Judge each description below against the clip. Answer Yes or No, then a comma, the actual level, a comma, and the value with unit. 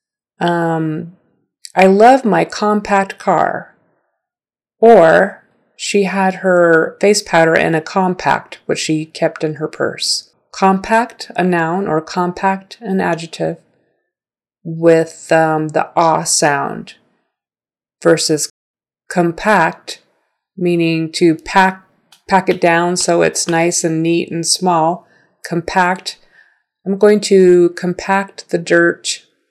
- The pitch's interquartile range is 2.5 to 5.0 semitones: Yes, average, 2.8 semitones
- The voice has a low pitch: No, medium, 175 Hz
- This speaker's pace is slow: Yes, slow, 110 wpm